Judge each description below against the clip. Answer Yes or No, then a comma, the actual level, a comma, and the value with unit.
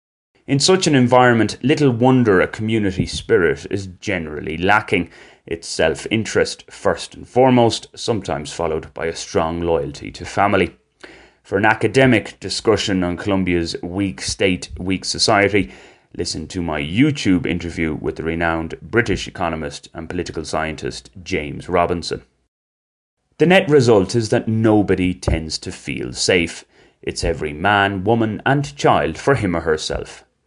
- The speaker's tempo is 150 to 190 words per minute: No, average, 140 wpm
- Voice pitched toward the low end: Yes, very low, 95 Hz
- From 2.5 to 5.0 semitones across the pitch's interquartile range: No, wide, 5.4 semitones